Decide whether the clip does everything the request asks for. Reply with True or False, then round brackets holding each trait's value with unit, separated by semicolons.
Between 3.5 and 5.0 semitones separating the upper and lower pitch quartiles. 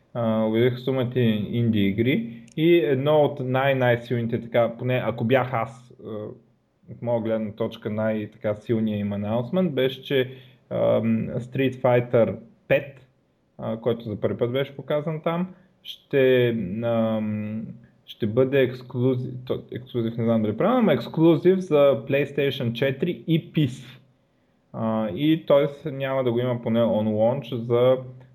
False (3.1 semitones)